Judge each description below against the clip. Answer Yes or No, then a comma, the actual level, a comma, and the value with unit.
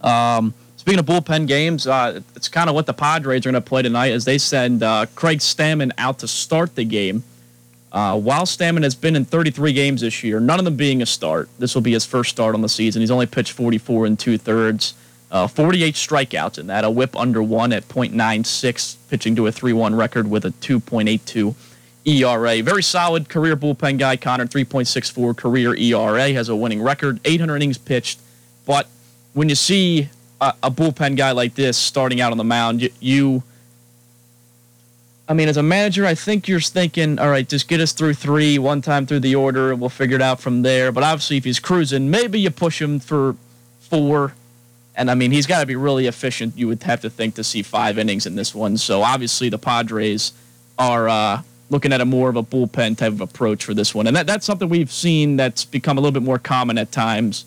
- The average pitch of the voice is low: Yes, low, 125 Hz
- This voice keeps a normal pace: No, fast, 215 wpm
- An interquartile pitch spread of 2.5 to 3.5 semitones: No, average, 4.2 semitones